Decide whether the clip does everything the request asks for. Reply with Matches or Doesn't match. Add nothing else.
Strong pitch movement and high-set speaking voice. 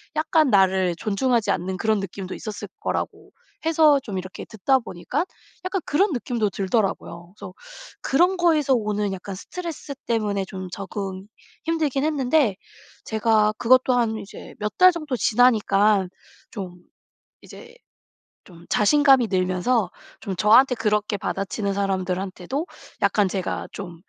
Matches